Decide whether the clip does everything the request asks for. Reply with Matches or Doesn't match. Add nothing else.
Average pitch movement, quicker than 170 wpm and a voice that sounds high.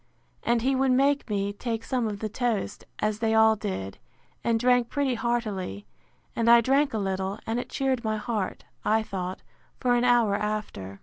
Matches